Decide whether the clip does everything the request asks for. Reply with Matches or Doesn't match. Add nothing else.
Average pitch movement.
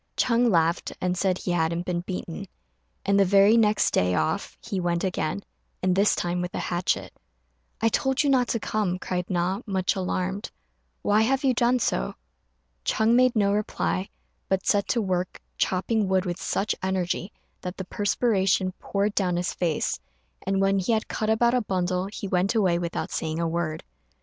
Matches